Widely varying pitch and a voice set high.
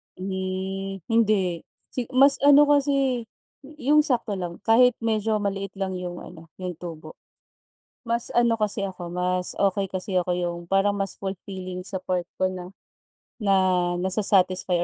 No: average, 3.7 semitones; high, 195 Hz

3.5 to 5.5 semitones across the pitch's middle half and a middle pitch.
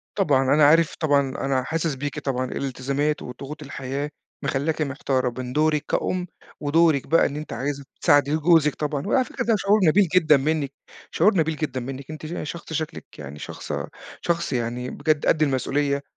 No: average, 2.9 semitones; medium, 145 Hz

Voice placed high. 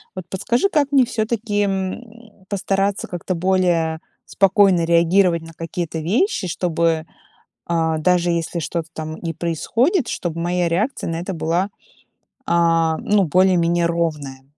No: medium, 175 Hz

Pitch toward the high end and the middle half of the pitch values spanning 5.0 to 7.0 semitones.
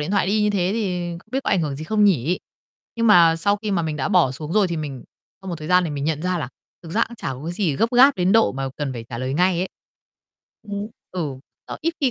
No: medium, 175 Hz; average, 5.3 semitones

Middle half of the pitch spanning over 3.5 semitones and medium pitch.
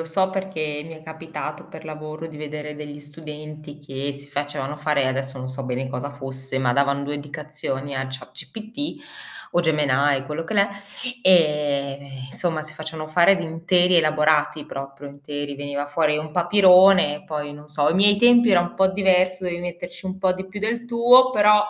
Yes: average, 4.0 semitones; medium, 150 Hz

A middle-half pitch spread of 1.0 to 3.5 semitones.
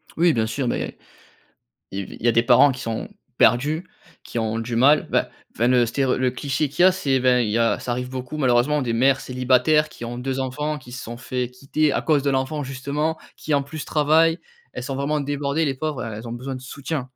Yes: average, 3.2 semitones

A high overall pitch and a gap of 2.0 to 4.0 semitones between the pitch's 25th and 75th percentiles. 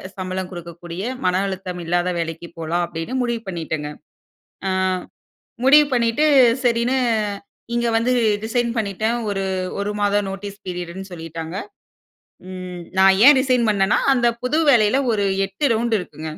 No: high, 195 Hz; average, 4.9 semitones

